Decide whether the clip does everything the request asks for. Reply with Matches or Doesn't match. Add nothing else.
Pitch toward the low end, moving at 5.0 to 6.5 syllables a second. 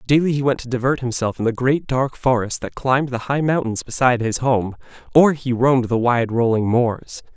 Matches